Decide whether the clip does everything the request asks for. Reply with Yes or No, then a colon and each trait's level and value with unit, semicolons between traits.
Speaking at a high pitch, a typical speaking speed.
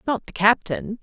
Yes: high, 220 Hz; average, 175 wpm